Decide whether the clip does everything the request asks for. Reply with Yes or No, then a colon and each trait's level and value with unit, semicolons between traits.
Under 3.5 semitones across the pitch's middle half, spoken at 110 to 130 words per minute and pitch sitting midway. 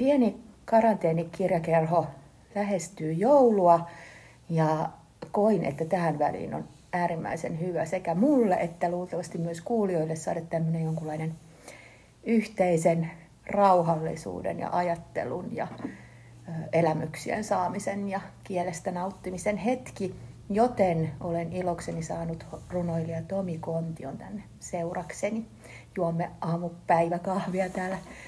No: average, 2.8 semitones; slow, 95 wpm; medium, 175 Hz